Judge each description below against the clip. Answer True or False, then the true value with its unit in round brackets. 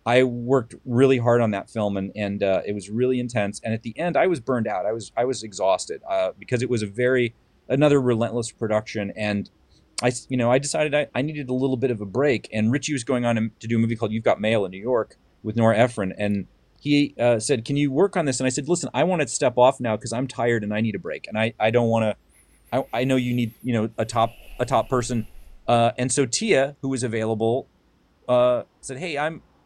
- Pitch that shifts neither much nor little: True (3.2 semitones)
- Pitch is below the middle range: True (120 Hz)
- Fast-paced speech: True (255 wpm)